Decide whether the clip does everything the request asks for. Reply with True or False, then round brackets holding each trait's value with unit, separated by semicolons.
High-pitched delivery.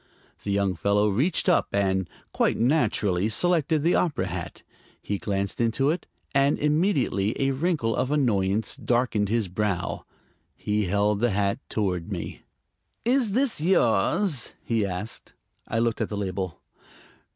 False (110 Hz)